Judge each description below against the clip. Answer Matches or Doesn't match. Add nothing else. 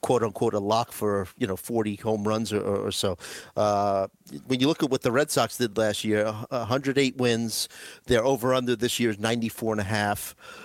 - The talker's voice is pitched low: Matches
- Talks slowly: Doesn't match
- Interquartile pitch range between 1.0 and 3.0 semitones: Matches